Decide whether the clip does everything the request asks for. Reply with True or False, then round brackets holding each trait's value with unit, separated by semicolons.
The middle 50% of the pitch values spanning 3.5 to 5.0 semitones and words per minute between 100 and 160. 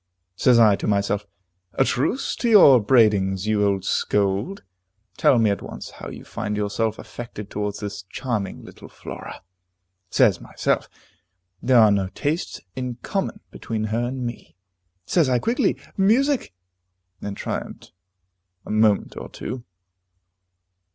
True (4.1 semitones; 140 wpm)